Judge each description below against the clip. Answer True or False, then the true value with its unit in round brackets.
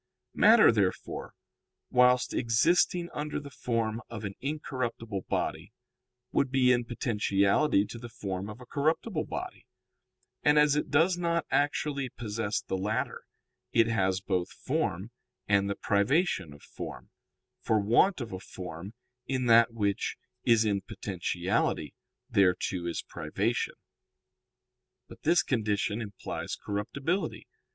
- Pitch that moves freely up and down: True (5.8 semitones)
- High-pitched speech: False (115 Hz)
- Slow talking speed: True (130 wpm)